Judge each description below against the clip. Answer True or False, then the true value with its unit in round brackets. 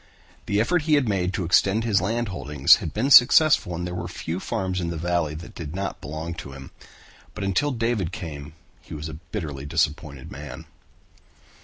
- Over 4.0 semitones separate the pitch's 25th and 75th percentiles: True (5.1 semitones)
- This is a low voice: True (90 Hz)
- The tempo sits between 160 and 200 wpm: True (190 wpm)